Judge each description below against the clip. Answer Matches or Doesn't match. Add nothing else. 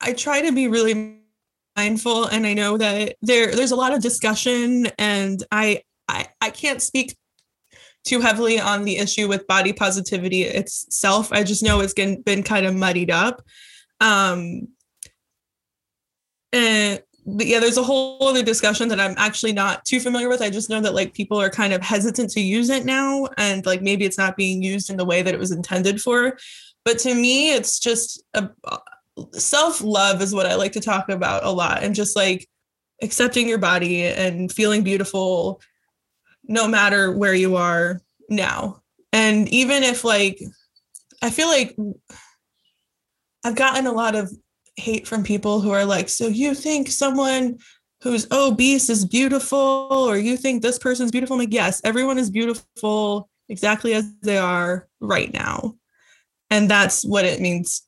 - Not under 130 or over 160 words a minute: Doesn't match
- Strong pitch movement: Doesn't match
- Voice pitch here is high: Matches